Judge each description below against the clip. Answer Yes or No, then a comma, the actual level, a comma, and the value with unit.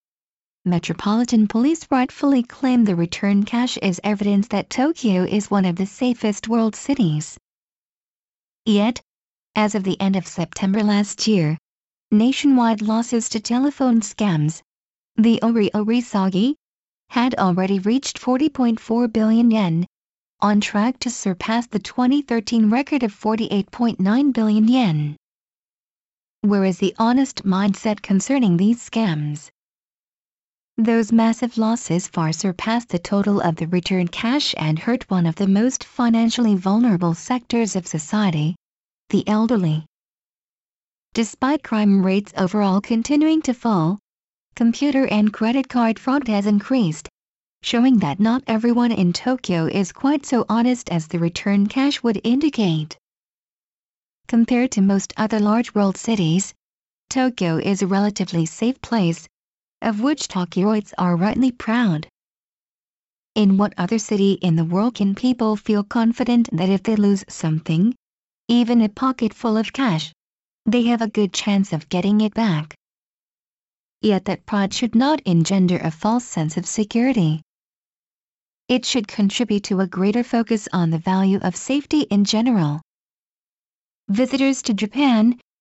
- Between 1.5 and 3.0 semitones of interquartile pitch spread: No, average, 3.9 semitones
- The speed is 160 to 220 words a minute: No, slow, 135 wpm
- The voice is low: No, high, 215 Hz